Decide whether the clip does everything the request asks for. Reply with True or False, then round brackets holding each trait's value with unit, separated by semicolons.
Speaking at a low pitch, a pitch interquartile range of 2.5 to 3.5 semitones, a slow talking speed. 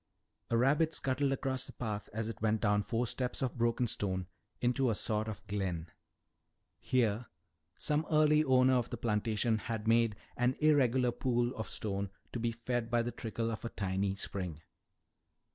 False (115 Hz; 3.2 semitones; 170 wpm)